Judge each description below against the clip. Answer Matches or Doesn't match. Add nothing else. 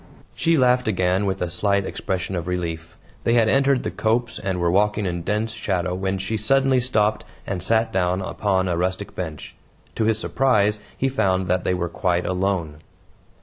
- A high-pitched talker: Doesn't match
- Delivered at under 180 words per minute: Doesn't match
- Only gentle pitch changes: Doesn't match